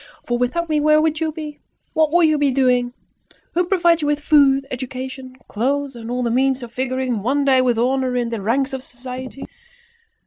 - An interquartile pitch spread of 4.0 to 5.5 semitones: No, average, 3.0 semitones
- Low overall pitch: No, very high, 265 Hz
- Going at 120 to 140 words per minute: No, average, 200 wpm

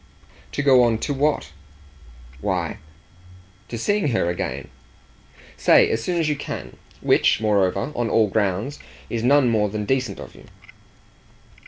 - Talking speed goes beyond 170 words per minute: No, average, 145 wpm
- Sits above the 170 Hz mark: No, low, 115 Hz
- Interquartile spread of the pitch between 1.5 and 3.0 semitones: No, average, 5.2 semitones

